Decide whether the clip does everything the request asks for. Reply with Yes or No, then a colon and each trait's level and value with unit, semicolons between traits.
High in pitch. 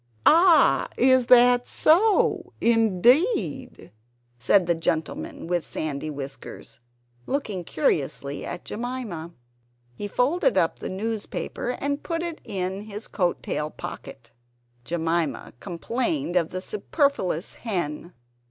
Yes: high, 210 Hz